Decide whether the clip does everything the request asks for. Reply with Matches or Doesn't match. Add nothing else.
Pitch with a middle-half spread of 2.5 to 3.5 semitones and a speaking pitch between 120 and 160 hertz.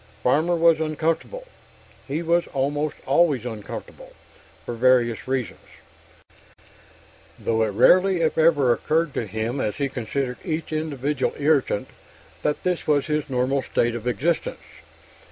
Doesn't match